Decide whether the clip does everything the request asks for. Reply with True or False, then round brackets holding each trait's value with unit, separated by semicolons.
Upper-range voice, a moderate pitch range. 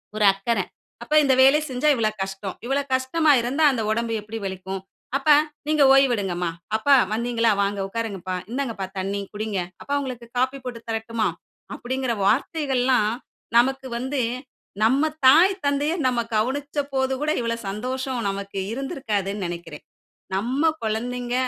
True (240 Hz; 4.1 semitones)